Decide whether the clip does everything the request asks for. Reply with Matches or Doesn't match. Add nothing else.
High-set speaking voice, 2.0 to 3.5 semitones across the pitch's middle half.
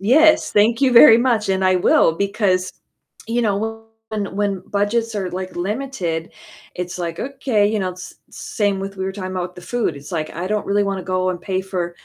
Matches